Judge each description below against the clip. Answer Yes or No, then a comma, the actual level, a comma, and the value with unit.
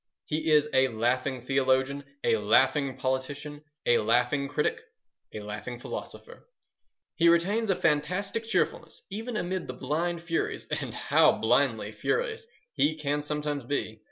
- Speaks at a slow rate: Yes, slow, 130 wpm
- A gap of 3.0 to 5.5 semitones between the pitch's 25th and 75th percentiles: Yes, average, 4.6 semitones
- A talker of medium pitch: Yes, medium, 145 Hz